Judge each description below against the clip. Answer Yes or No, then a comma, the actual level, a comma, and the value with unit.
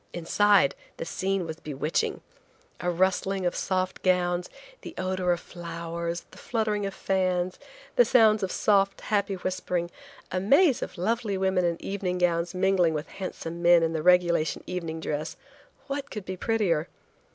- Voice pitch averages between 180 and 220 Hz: Yes, medium, 185 Hz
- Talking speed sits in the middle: Yes, average, 150 wpm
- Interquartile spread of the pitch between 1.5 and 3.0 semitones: Yes, narrow, 2.4 semitones